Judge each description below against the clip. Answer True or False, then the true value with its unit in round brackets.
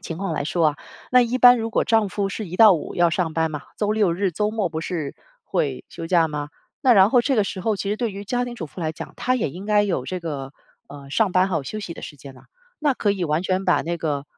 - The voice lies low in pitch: False (185 Hz)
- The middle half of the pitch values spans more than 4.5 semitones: True (5.0 semitones)